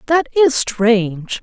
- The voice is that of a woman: Yes, female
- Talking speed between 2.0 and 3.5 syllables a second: Yes, 3.4 syllables/s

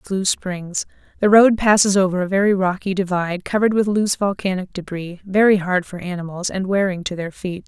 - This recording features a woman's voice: Yes, female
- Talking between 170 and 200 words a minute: Yes, average, 180 wpm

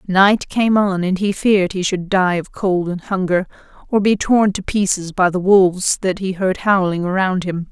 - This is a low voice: No, high, 190 Hz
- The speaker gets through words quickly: Yes, fast, 210 wpm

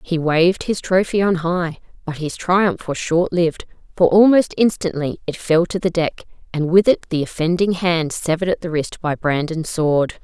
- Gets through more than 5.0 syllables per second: No, 4.8 syllables/s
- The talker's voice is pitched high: No, medium, 170 Hz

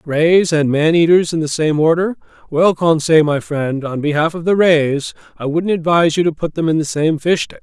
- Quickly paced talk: Yes, fast, 230 wpm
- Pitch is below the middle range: No, medium, 160 Hz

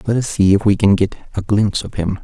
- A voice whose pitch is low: Yes, low, 105 Hz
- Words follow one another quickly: Yes, fast, 295 wpm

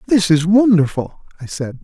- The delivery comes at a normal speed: Yes, average, 165 wpm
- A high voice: No, medium, 175 Hz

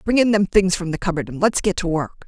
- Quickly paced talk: Yes, fast, 315 wpm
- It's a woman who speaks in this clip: Yes, female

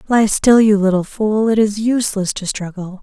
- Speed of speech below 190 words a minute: No, average, 200 wpm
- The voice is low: No, high, 210 Hz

